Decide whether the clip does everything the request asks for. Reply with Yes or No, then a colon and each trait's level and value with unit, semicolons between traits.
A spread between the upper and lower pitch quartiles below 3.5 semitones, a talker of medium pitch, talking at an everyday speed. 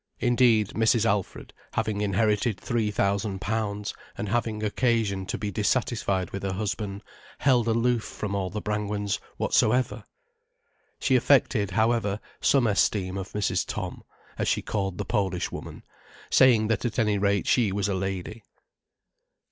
No: narrow, 2.4 semitones; low, 105 Hz; average, 145 wpm